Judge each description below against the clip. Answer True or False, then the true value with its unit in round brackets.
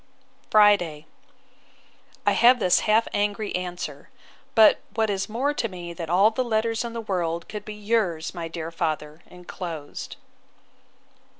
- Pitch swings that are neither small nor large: True (4.4 semitones)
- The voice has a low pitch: False (195 Hz)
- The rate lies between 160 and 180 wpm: False (140 wpm)